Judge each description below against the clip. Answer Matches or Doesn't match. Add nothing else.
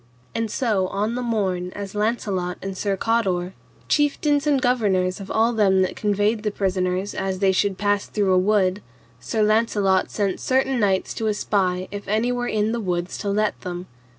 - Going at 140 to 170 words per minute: Doesn't match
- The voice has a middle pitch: Doesn't match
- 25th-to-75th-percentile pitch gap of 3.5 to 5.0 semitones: Doesn't match